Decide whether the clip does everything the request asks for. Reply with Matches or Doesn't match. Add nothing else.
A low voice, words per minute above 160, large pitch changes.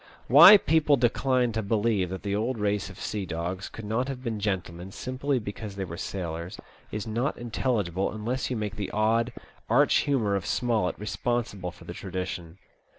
Doesn't match